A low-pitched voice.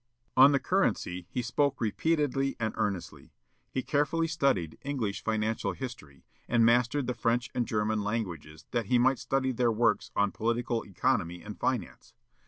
Yes: low, 120 Hz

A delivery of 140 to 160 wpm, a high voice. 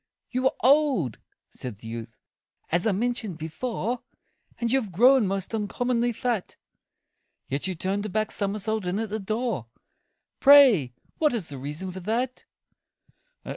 Yes: average, 150 wpm; high, 215 Hz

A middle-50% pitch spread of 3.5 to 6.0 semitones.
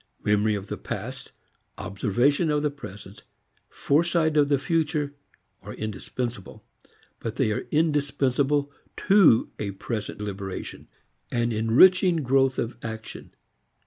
Yes: wide, 5.5 semitones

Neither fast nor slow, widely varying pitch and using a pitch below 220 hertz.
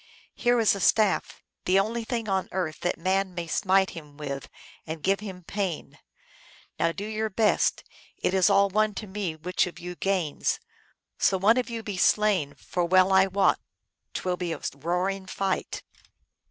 No: average, 180 wpm; average, 2.7 semitones; high, 190 Hz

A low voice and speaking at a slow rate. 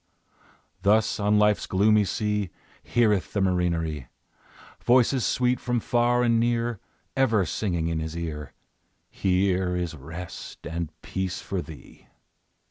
Yes: very low, 95 Hz; slow, 125 wpm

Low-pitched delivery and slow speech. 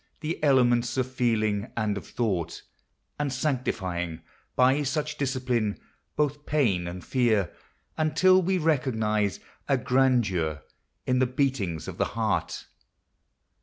Yes: low, 125 Hz; slow, 130 wpm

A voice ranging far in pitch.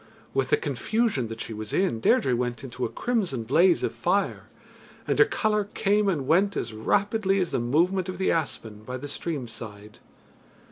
Yes: wide, 8.8 semitones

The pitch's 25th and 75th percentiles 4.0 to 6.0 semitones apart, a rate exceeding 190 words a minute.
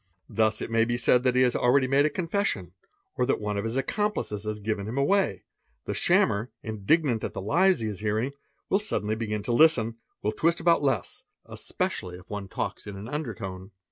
Yes: average, 5.0 semitones; average, 200 wpm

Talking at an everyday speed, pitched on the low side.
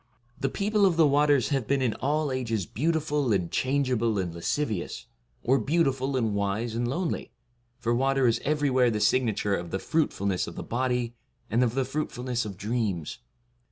Yes: average, 175 wpm; low, 125 Hz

